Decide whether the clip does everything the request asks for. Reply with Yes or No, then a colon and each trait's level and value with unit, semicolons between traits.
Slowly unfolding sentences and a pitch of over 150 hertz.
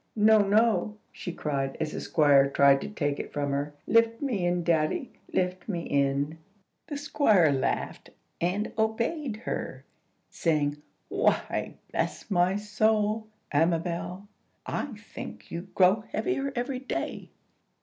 Yes: slow, 130 wpm; medium, 185 Hz